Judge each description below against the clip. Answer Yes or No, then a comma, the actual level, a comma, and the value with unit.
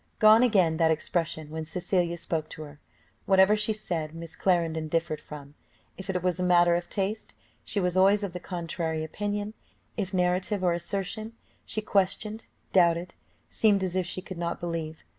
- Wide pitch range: No, average, 3.0 semitones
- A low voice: No, medium, 180 Hz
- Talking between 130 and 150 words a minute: No, average, 175 wpm